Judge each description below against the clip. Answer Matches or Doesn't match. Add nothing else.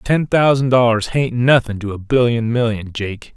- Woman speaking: Doesn't match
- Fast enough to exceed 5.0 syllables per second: Doesn't match